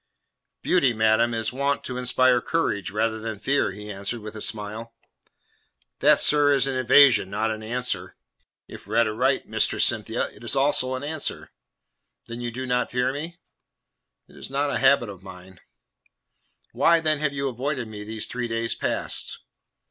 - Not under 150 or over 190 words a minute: Yes, average, 170 wpm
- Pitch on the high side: No, low, 120 Hz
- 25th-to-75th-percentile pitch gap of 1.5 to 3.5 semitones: No, average, 4.0 semitones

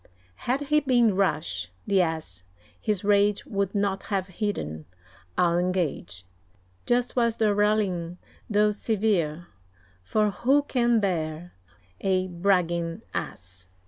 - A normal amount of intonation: Yes, average, 4.0 semitones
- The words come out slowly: Yes, slow, 115 wpm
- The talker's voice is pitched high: Yes, high, 195 Hz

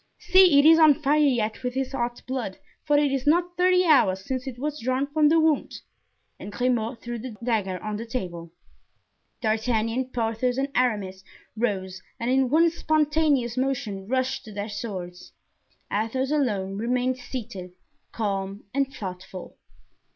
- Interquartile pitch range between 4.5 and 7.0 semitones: Yes, average, 4.8 semitones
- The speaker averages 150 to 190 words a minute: Yes, average, 155 wpm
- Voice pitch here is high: Yes, very high, 250 Hz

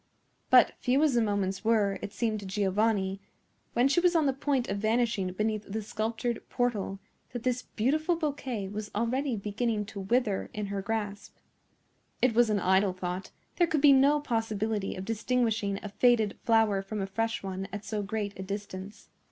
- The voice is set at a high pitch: Yes, high, 215 Hz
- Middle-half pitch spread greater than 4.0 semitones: No, average, 3.4 semitones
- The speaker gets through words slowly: No, average, 180 wpm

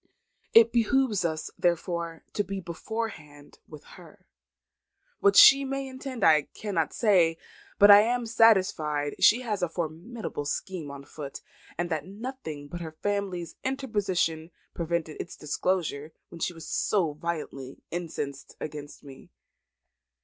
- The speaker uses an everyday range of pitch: No, wide, 5.9 semitones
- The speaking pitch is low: No, medium, 175 Hz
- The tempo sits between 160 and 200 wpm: No, slow, 135 wpm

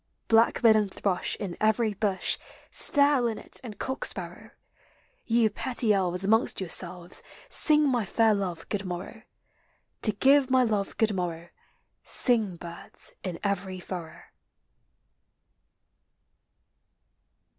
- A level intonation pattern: No, average, 4.1 semitones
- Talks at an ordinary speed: No, slow, 115 wpm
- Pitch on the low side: No, high, 205 Hz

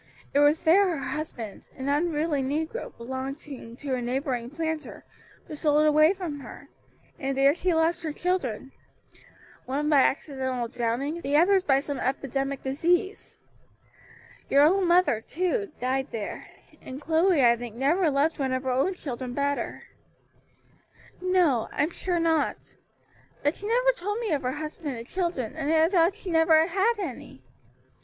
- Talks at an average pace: Yes, average, 160 wpm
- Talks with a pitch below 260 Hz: No, very high, 295 Hz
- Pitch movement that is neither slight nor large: Yes, average, 4.4 semitones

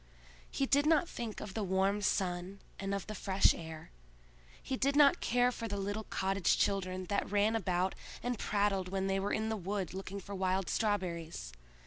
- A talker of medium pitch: No, high, 200 Hz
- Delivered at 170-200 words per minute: Yes, average, 185 wpm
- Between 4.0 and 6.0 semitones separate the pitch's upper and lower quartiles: No, narrow, 2.5 semitones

